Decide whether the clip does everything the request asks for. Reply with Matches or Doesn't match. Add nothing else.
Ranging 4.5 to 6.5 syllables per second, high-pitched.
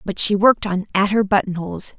Matches